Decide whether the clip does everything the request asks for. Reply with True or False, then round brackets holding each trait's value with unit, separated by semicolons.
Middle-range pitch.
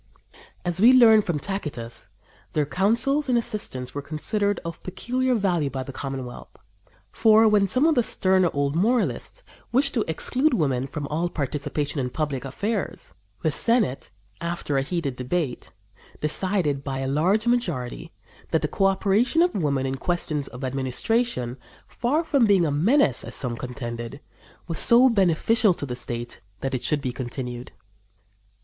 True (165 Hz)